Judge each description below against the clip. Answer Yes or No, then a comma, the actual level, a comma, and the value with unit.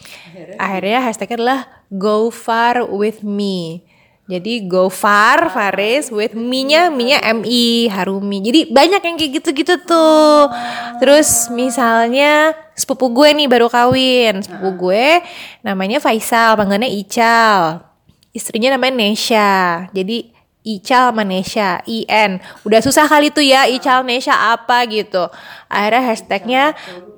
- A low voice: No, high, 230 Hz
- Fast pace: No, average, 120 wpm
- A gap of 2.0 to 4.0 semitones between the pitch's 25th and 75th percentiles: No, average, 4.8 semitones